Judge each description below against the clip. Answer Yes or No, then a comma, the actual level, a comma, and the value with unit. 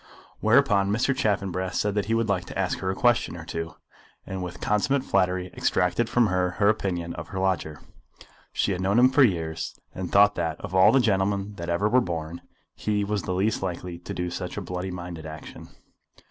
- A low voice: Yes, very low, 95 Hz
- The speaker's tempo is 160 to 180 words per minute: No, fast, 205 wpm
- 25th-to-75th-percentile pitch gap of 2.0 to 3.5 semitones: Yes, average, 2.8 semitones